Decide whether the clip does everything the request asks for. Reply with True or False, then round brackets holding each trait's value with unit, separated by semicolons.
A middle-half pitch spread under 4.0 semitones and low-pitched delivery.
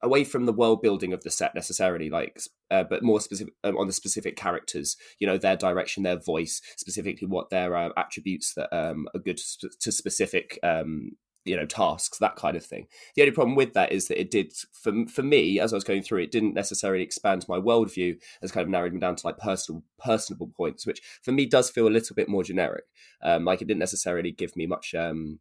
False (4.5 semitones; 95 Hz)